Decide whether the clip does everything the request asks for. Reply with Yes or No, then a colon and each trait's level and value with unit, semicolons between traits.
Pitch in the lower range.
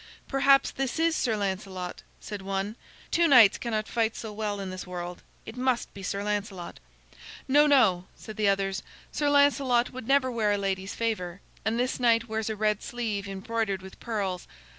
No: high, 215 Hz